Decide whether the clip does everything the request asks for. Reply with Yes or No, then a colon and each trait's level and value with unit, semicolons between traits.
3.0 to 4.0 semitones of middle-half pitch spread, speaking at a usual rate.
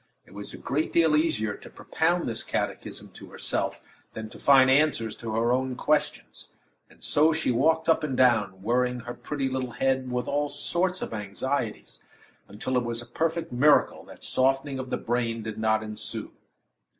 No: average, 4.4 semitones; average, 180 wpm